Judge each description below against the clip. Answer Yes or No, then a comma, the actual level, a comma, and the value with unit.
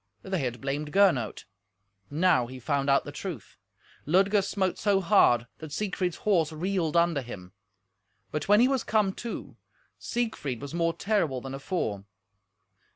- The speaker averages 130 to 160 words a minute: Yes, average, 150 wpm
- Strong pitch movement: Yes, wide, 6.2 semitones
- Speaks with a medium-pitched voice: Yes, medium, 165 Hz